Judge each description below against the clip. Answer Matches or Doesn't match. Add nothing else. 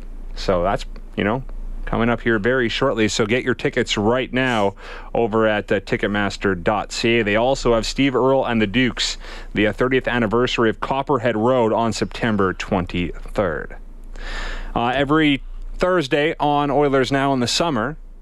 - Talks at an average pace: Matches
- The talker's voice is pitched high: Doesn't match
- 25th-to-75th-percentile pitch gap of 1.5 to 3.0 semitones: Doesn't match